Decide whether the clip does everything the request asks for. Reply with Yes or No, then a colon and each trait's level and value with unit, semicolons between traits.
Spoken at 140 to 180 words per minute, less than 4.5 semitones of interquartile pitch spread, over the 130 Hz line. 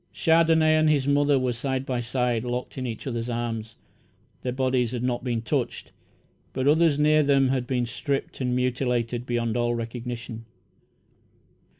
No: average, 160 wpm; narrow, 2.5 semitones; low, 125 Hz